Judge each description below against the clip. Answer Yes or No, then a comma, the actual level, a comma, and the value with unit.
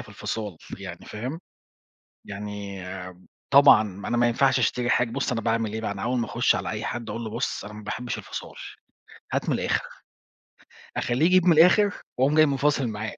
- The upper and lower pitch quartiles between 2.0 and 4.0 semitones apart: No, average, 4.5 semitones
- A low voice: Yes, low, 120 Hz